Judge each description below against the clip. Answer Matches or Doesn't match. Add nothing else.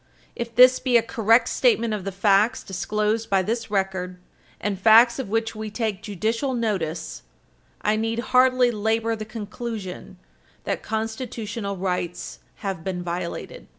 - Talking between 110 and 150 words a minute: Matches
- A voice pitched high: Matches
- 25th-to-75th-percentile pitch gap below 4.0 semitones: Matches